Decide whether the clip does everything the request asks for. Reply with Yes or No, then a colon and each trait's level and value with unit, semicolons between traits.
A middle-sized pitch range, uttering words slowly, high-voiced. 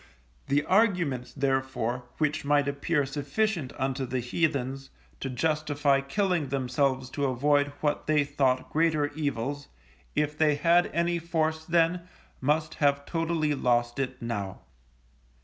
No: average, 3.1 semitones; slow, 130 wpm; medium, 145 Hz